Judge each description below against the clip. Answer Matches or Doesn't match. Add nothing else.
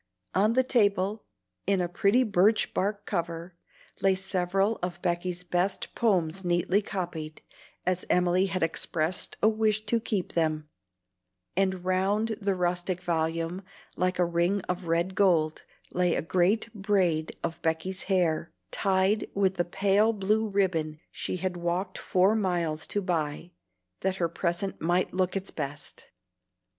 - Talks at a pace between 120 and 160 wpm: Matches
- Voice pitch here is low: Doesn't match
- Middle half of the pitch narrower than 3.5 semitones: Matches